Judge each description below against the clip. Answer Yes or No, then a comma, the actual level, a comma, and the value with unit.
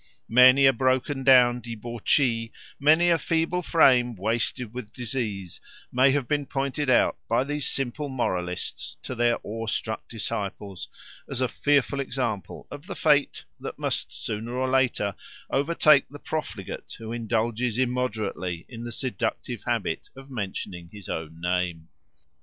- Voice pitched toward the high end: No, low, 125 Hz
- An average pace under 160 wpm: Yes, average, 140 wpm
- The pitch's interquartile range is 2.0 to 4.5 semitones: Yes, average, 3.9 semitones